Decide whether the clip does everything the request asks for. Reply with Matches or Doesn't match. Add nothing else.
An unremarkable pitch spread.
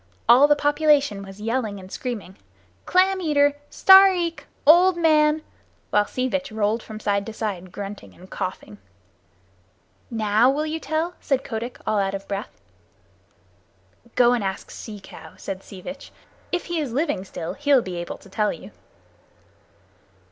Doesn't match